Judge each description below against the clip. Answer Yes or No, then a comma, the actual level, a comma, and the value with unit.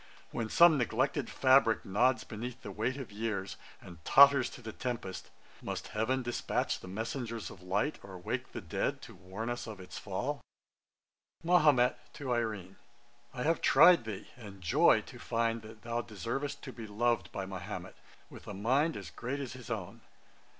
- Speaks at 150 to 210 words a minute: Yes, average, 170 wpm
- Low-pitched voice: Yes, low, 115 Hz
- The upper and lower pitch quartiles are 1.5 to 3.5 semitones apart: No, average, 4.0 semitones